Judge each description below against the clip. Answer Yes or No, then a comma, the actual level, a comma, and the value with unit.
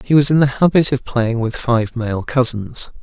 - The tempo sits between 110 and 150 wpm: No, fast, 220 wpm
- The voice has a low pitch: Yes, low, 125 Hz